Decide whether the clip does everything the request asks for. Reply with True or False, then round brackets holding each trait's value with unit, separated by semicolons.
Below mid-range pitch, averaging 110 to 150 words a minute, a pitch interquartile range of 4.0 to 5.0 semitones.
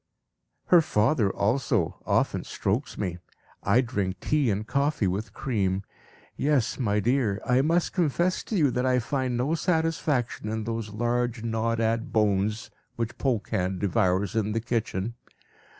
True (115 Hz; 145 wpm; 4.3 semitones)